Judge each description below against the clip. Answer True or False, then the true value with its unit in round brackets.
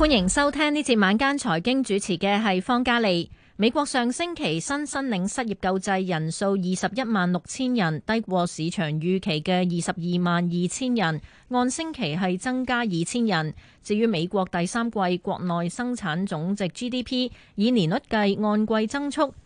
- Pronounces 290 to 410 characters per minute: False (260 characters per minute)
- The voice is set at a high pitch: True (205 Hz)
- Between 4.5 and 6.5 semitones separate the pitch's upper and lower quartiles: True (5.4 semitones)